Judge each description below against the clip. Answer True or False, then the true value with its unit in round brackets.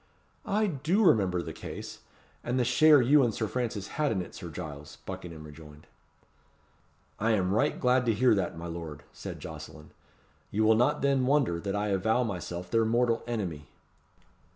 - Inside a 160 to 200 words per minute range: True (175 wpm)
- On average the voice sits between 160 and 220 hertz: False (110 Hz)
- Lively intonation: True (6.3 semitones)